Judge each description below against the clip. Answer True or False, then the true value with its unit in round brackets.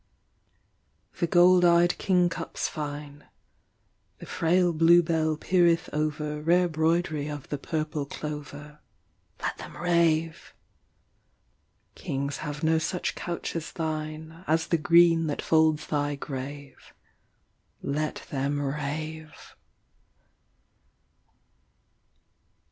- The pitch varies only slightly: True (2.2 semitones)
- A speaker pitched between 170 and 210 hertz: False (155 Hz)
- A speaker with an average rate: False (100 wpm)